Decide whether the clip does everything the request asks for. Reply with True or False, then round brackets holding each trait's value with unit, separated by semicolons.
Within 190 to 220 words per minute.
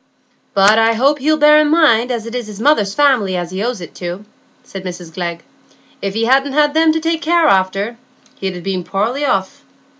True (200 wpm)